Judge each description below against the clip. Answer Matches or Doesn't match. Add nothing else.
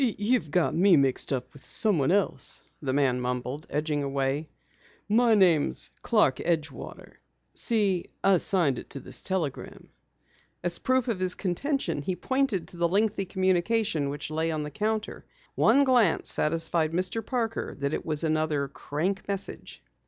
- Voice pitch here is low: Doesn't match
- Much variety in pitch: Matches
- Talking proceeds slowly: Doesn't match